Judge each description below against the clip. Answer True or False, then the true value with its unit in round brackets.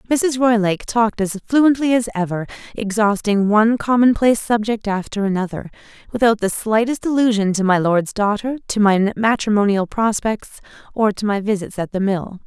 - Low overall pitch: False (215 Hz)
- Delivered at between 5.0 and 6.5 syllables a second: True (5.3 syllables/s)